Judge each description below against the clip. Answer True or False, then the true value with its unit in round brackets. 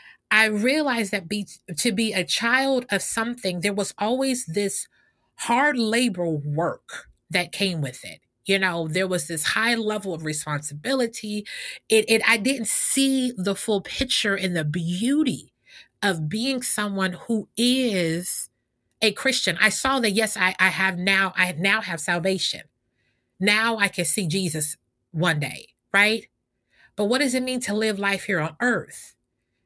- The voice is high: True (200 Hz)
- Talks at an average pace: True (160 wpm)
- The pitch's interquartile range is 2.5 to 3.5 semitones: False (4.7 semitones)